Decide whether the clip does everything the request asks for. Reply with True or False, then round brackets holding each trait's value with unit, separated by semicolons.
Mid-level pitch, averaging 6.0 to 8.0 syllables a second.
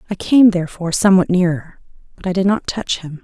True (180 Hz; 6.3 syllables/s)